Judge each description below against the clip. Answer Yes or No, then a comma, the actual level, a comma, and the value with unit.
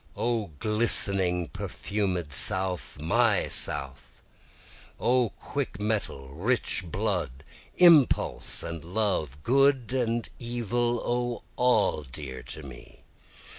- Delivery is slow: Yes, slow, 95 wpm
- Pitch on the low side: Yes, low, 105 Hz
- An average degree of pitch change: No, wide, 7.3 semitones